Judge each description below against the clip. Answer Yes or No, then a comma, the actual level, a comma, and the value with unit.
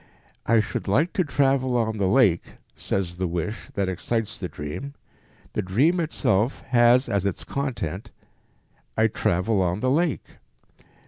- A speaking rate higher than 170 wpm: No, average, 145 wpm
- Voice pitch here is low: Yes, low, 110 Hz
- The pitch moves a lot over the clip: Yes, wide, 5.9 semitones